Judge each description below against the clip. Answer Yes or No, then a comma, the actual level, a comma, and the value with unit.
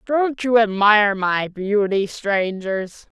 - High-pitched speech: Yes, high, 210 Hz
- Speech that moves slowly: Yes, slow, 115 wpm